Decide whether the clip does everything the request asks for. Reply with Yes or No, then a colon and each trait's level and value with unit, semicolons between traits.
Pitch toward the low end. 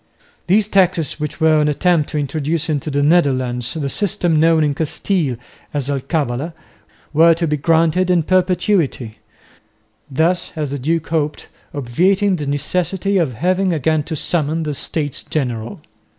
No: medium, 155 Hz